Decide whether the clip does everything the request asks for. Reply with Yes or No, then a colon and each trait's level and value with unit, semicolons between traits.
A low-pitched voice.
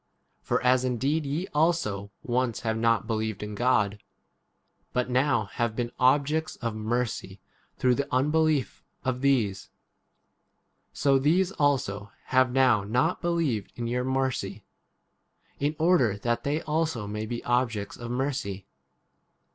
Yes: low, 125 Hz